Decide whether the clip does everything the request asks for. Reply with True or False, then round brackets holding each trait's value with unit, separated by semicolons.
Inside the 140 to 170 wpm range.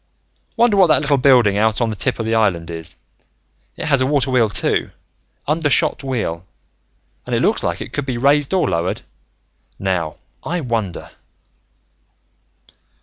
True (155 wpm)